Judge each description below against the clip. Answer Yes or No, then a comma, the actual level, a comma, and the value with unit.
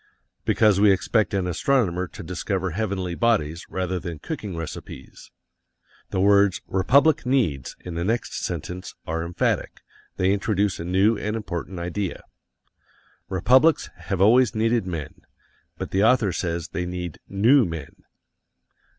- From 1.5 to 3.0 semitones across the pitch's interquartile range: No, average, 3.8 semitones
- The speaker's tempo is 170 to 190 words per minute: No, slow, 135 wpm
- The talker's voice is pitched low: Yes, very low, 95 Hz